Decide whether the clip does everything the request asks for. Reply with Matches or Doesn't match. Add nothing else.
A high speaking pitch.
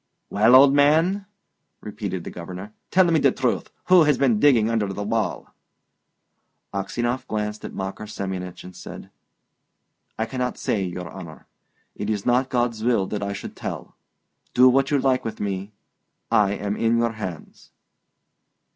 Doesn't match